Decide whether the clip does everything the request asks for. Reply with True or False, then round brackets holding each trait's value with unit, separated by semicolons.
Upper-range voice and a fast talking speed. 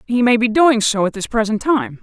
True (235 Hz; 265 wpm)